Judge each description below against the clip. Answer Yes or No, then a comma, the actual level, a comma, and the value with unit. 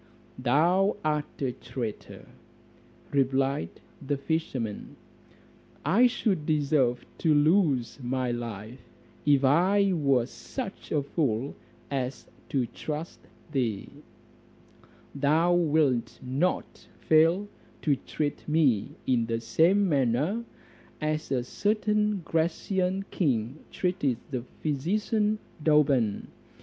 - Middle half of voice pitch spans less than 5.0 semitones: No, wide, 5.4 semitones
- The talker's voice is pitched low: No, medium, 145 Hz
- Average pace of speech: No, slow, 100 wpm